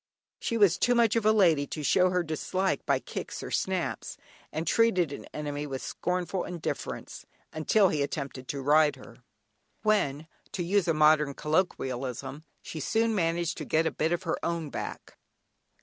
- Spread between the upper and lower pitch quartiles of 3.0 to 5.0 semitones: Yes, average, 4.0 semitones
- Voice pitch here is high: No, medium, 165 Hz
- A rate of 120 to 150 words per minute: No, average, 170 wpm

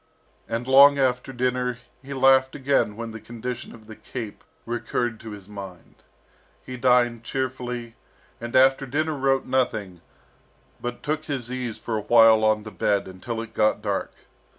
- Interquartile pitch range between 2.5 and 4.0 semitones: Yes, average, 3.1 semitones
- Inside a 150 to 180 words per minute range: Yes, average, 160 wpm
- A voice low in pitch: Yes, low, 120 Hz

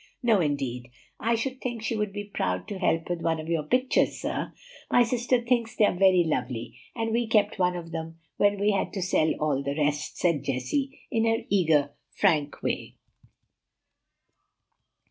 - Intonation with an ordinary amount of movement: No, wide, 6.8 semitones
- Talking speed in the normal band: Yes, average, 180 wpm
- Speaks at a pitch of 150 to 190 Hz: Yes, medium, 185 Hz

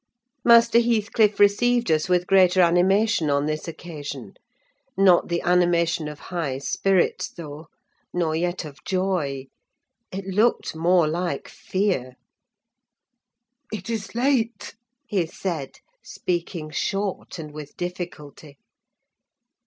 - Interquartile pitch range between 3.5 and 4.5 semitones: Yes, average, 4.0 semitones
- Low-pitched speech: No, medium, 175 Hz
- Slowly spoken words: Yes, slow, 110 wpm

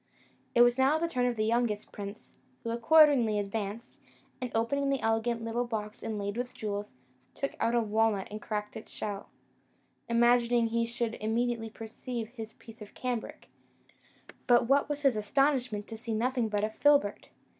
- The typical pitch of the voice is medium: No, high, 230 Hz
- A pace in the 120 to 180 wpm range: Yes, average, 165 wpm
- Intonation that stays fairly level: Yes, narrow, 2.3 semitones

